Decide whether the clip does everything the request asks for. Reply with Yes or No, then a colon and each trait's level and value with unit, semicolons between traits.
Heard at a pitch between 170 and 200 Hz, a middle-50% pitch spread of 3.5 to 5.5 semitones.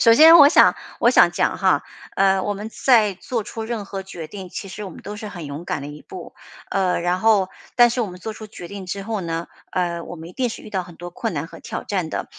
Yes: high, 195 Hz; average, 3.9 semitones